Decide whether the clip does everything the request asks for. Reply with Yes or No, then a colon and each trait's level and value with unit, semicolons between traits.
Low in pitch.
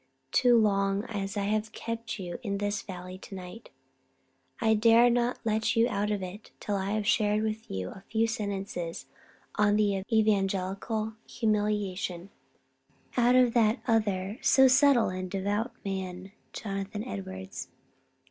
No: high, 210 Hz